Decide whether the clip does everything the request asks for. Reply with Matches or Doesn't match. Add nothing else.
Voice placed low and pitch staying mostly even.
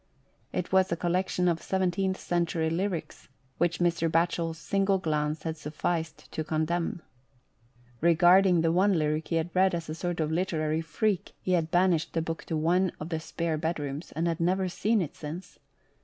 Doesn't match